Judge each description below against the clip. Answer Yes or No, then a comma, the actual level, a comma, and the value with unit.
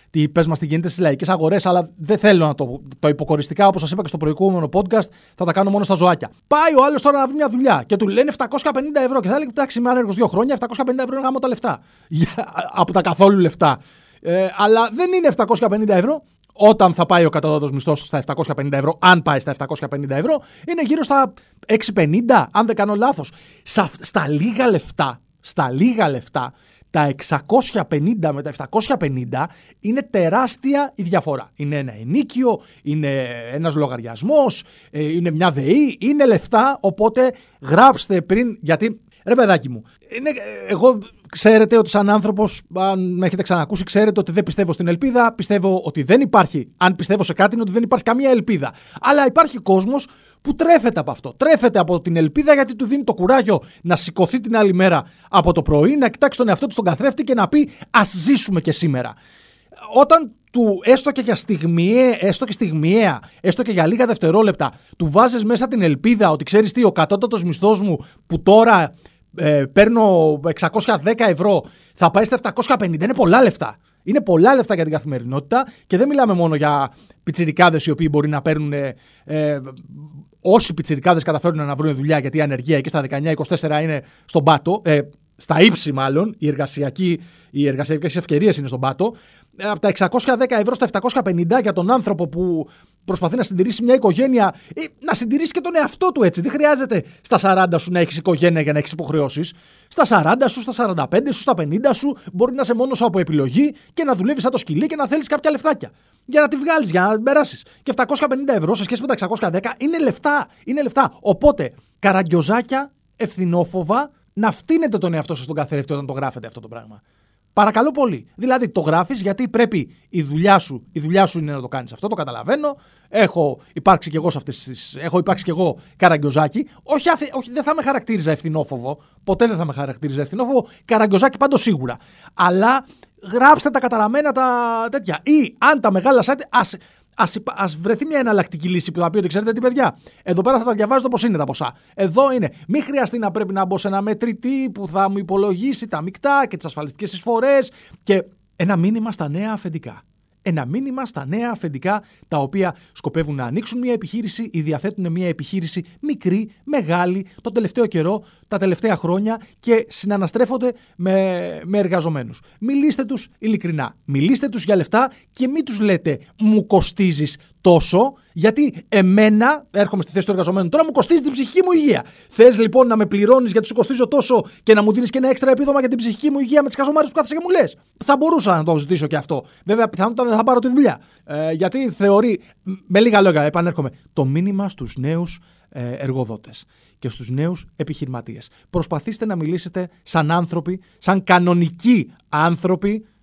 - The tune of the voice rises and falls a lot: Yes, wide, 7.1 semitones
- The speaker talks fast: Yes, fast, 185 wpm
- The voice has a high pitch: Yes, high, 195 Hz